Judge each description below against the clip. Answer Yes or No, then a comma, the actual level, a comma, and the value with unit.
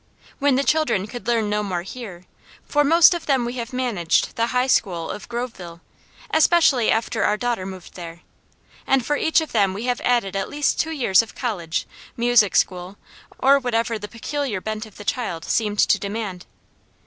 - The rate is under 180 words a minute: No, average, 185 wpm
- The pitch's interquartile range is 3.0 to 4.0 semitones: No, average, 4.6 semitones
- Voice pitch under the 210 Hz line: No, high, 230 Hz